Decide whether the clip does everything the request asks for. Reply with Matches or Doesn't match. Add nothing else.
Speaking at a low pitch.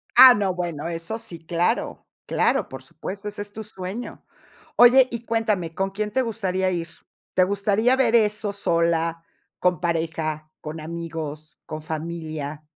Doesn't match